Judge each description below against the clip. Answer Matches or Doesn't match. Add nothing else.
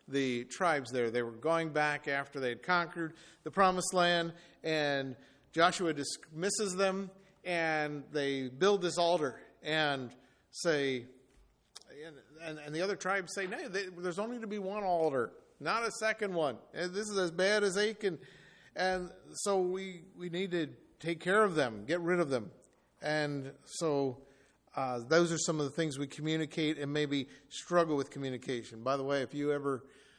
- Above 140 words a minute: Matches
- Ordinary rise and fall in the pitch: Matches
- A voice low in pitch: Doesn't match